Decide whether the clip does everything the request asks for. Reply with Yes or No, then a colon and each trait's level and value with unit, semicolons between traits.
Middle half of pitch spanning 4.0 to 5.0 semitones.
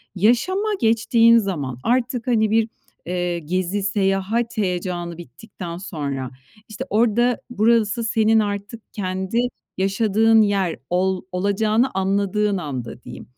No: average, 3.6 semitones